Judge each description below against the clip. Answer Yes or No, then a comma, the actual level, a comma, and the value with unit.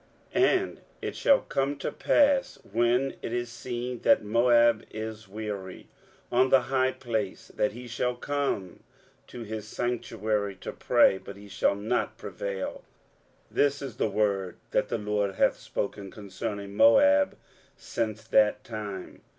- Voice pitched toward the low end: Yes, low, 110 Hz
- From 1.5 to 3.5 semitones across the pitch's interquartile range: Yes, average, 3.2 semitones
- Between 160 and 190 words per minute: No, average, 150 wpm